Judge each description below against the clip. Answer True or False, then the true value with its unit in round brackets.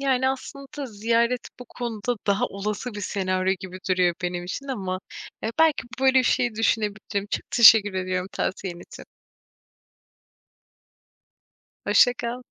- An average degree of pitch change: True (4.8 semitones)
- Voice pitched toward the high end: True (215 Hz)